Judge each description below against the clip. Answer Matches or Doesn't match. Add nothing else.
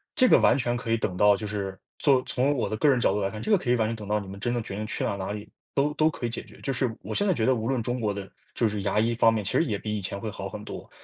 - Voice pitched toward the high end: Doesn't match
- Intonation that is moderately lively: Matches